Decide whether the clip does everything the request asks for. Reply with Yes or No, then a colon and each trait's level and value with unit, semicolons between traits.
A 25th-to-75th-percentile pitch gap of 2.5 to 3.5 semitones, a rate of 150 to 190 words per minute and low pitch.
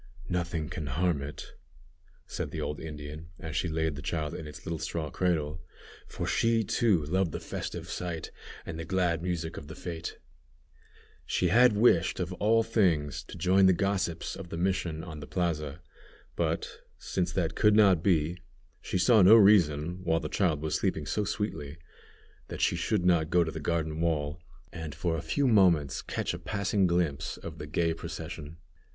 Yes: average, 3.1 semitones; average, 180 wpm; very low, 85 Hz